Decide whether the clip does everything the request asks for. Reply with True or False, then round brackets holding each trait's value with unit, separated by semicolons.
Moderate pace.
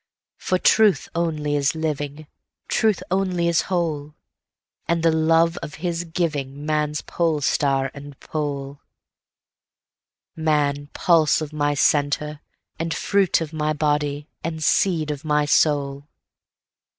False (105 wpm)